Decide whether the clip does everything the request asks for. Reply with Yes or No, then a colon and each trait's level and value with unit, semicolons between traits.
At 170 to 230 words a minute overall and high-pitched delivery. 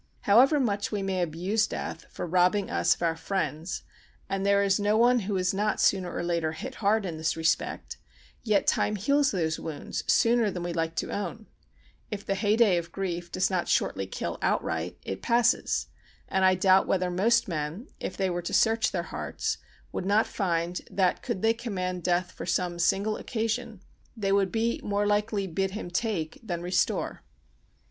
Yes: average, 185 wpm; high, 195 Hz